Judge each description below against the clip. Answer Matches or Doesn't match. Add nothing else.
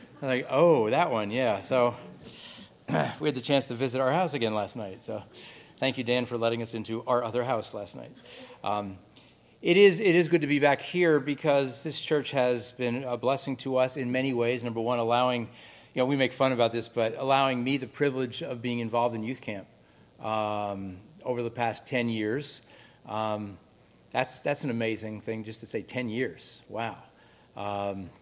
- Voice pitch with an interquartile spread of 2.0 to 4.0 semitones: Matches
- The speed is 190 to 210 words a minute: Matches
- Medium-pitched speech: Doesn't match